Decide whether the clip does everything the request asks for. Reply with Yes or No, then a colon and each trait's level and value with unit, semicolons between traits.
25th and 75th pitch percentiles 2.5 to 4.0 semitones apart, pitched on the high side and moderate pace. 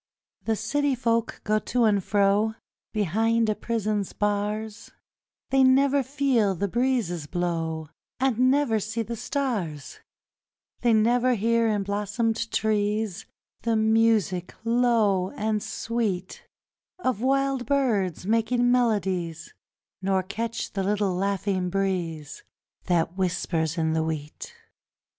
No: average, 3.6 semitones; high, 215 Hz; slow, 115 wpm